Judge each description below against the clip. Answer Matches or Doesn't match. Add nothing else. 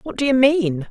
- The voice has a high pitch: Matches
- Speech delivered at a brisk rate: Matches